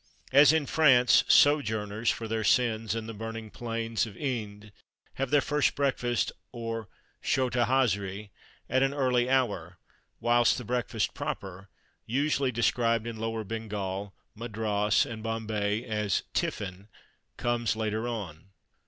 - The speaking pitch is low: Yes, low, 115 Hz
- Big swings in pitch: No, average, 2.7 semitones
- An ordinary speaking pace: No, slow, 130 wpm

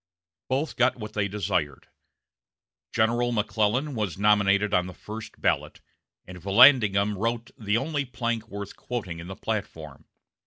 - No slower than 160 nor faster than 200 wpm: No, average, 140 wpm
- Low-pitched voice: Yes, low, 105 Hz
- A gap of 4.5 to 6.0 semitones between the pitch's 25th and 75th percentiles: No, average, 3.2 semitones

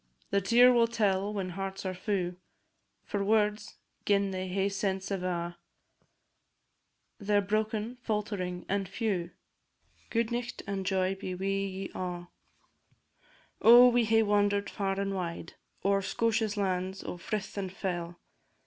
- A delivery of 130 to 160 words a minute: Yes, average, 140 wpm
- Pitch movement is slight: Yes, narrow, 2.2 semitones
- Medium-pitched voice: No, high, 195 Hz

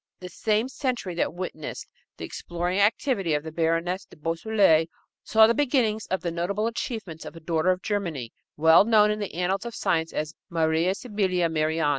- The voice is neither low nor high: Yes, medium, 180 Hz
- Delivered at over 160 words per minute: Yes, average, 180 wpm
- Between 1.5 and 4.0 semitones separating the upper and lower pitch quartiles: No, average, 4.4 semitones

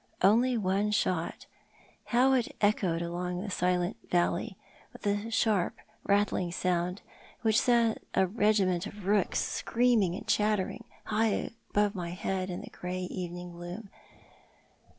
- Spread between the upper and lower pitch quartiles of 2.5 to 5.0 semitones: Yes, average, 3.2 semitones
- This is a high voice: Yes, high, 195 Hz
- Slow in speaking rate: Yes, slow, 130 wpm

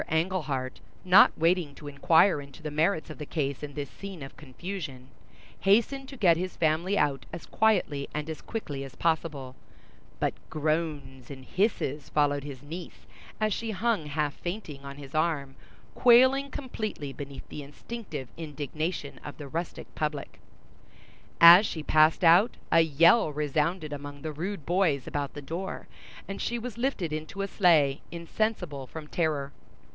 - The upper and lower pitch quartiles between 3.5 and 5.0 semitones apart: Yes, average, 4.4 semitones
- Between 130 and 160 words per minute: Yes, average, 155 wpm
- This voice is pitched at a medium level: Yes, medium, 155 Hz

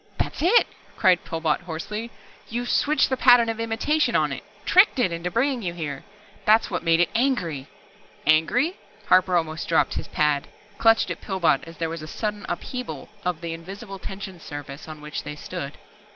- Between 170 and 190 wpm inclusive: Yes, average, 180 wpm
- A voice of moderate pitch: Yes, medium, 180 Hz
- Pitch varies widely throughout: Yes, wide, 6.1 semitones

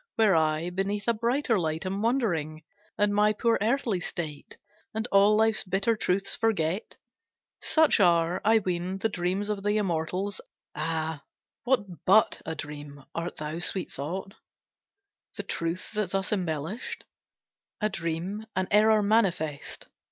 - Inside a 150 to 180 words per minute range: No, average, 140 wpm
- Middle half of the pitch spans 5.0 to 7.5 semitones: No, average, 4.3 semitones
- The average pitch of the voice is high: Yes, high, 195 Hz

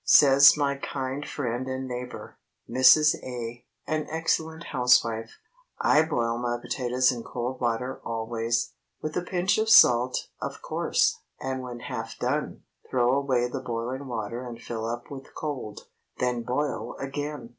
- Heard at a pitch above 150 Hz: No, low, 125 Hz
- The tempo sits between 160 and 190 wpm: No, average, 140 wpm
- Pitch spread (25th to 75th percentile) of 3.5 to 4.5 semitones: No, average, 3.0 semitones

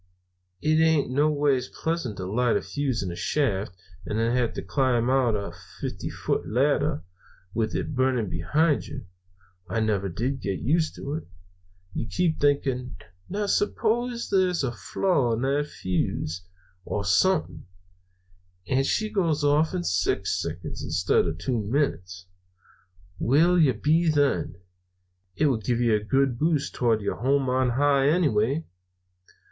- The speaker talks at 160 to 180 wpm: No, average, 150 wpm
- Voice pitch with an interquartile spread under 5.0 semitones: No, wide, 5.6 semitones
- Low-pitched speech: Yes, low, 130 Hz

